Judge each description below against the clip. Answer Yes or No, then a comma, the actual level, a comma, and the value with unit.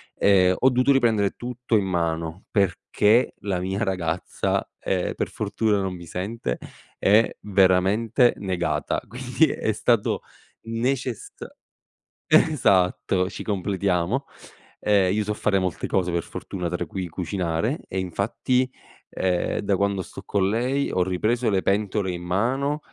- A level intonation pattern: No, average, 3.9 semitones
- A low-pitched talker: Yes, low, 100 Hz